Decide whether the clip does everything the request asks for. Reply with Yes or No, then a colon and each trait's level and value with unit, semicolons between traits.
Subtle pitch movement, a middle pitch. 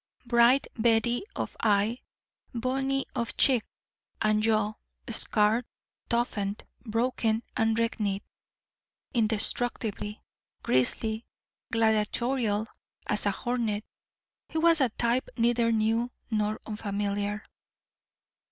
No: narrow, 2.2 semitones; high, 225 Hz